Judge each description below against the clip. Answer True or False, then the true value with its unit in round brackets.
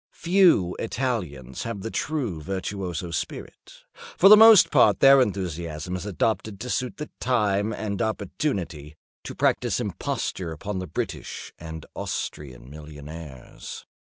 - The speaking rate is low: True (125 wpm)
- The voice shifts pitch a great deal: True (6.4 semitones)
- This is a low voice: True (95 Hz)